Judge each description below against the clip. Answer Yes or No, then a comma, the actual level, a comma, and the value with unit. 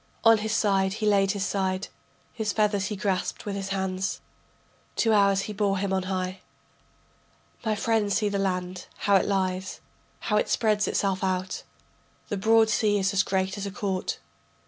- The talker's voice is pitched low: No, high, 195 Hz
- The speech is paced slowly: No, average, 175 wpm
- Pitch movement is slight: Yes, narrow, 1.7 semitones